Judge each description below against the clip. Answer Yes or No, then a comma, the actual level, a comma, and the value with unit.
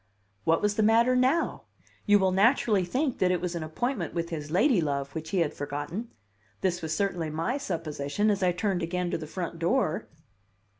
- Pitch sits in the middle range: Yes, medium, 180 Hz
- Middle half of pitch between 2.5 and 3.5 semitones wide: No, average, 4.7 semitones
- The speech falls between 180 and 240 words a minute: Yes, average, 190 wpm